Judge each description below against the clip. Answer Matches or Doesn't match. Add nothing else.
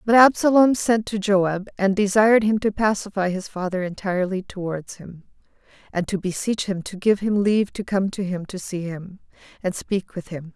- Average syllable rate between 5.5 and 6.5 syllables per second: Doesn't match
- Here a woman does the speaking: Matches